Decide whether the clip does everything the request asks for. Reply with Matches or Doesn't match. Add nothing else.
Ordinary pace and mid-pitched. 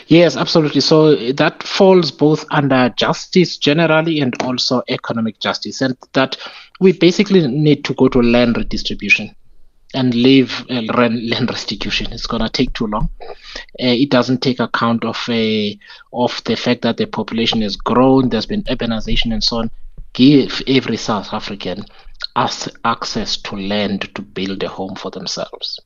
Doesn't match